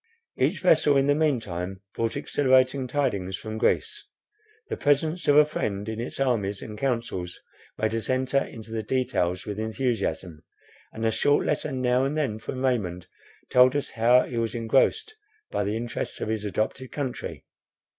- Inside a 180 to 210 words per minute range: No, average, 170 wpm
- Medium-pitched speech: No, low, 120 Hz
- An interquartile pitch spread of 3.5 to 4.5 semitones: Yes, average, 4.0 semitones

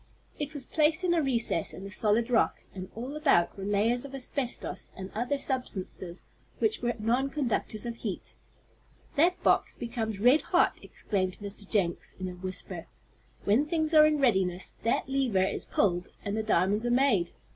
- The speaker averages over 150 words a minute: Yes, average, 170 wpm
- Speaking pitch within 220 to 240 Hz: Yes, high, 230 Hz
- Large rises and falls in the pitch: Yes, wide, 5.9 semitones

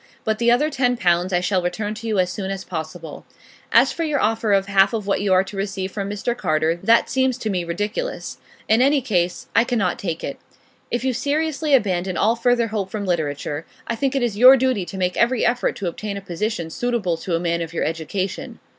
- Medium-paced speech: No, fast, 225 wpm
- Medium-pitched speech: No, high, 200 Hz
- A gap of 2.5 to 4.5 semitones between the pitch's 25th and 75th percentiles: No, average, 5.0 semitones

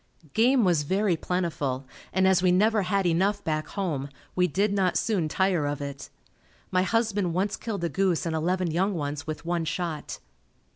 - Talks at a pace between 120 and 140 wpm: No, average, 180 wpm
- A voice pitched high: No, medium, 180 Hz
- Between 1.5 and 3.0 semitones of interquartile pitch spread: No, average, 3.6 semitones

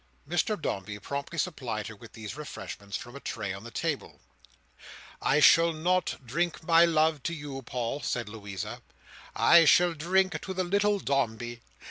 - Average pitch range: No, wide, 6.8 semitones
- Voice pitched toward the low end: No, medium, 145 Hz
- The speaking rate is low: No, average, 160 wpm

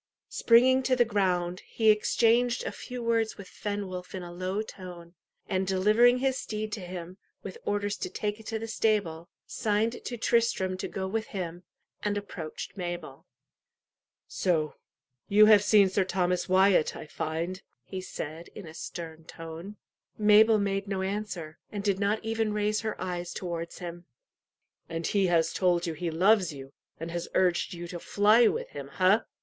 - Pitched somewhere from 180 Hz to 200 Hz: Yes, high, 190 Hz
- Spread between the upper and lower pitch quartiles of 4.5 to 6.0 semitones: No, average, 3.6 semitones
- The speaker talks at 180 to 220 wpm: No, average, 170 wpm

